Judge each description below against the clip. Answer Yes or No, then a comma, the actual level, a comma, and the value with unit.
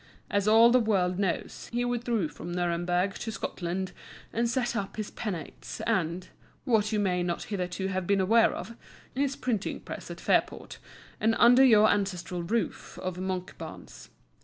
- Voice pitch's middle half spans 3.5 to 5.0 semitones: Yes, average, 4.2 semitones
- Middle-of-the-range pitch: No, high, 200 Hz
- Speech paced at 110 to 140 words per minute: No, average, 160 wpm